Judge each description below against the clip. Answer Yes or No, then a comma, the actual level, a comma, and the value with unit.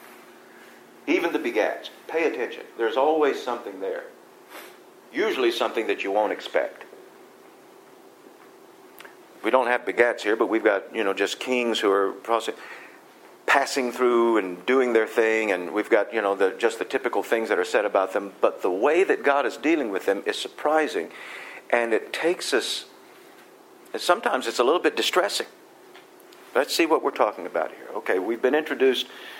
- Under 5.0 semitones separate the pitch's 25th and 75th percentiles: Yes, average, 3.7 semitones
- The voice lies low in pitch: No, very high, 390 Hz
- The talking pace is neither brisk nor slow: Yes, average, 170 wpm